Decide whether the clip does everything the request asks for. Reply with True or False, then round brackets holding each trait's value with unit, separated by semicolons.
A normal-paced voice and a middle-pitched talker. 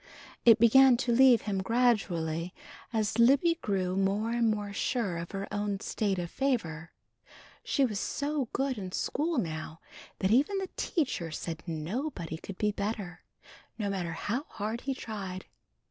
False (155 wpm; 210 Hz)